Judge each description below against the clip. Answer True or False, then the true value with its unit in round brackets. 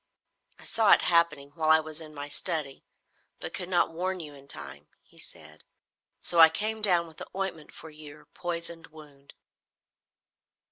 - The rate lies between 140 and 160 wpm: False (170 wpm)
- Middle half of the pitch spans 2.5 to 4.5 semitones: True (2.8 semitones)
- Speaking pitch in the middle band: True (160 Hz)